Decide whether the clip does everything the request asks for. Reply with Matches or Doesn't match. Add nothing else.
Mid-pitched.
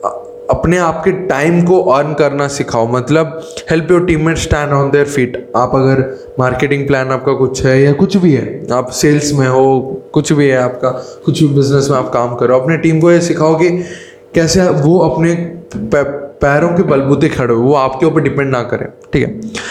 Matches